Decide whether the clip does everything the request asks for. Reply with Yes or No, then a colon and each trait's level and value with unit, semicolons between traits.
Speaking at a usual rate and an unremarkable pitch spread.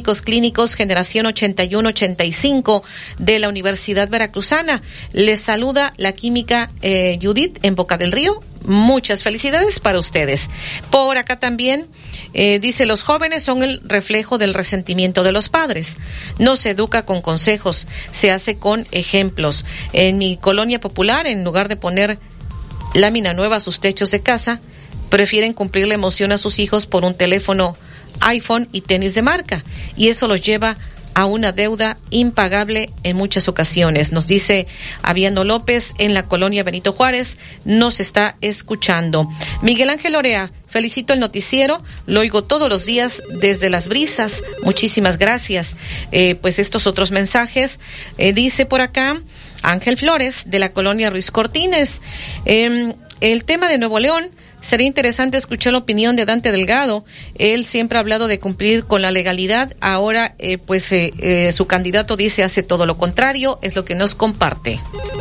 Yes: average, 155 wpm; average, 3.8 semitones